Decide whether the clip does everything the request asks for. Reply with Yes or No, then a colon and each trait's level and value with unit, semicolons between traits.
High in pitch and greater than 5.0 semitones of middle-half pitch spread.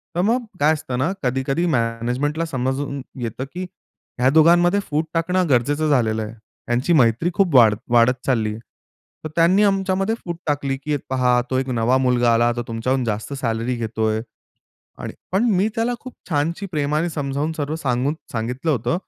No: low, 135 Hz; wide, 5.5 semitones